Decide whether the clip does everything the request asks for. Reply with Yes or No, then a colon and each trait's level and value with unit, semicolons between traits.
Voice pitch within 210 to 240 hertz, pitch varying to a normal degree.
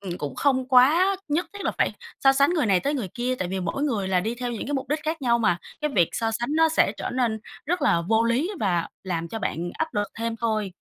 No: high, 235 Hz; wide, 6.4 semitones